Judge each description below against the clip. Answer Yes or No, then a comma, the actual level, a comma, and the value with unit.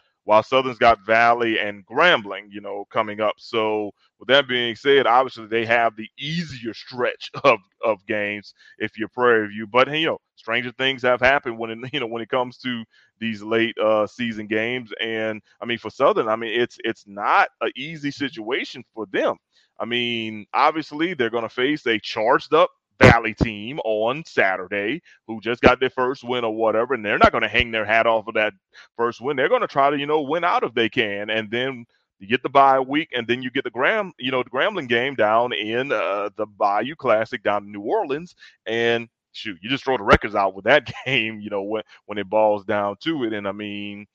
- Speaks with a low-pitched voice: Yes, low, 115 Hz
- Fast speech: Yes, fast, 215 wpm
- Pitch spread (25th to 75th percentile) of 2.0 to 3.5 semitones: Yes, average, 2.8 semitones